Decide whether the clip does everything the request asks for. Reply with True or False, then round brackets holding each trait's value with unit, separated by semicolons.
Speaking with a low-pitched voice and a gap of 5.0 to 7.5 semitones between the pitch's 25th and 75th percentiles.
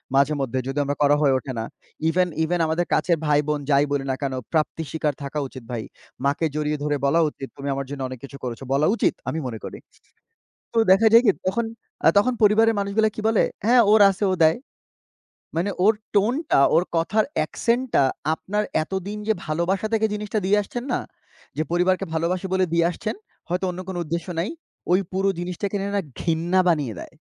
False (175 Hz; 5.6 semitones)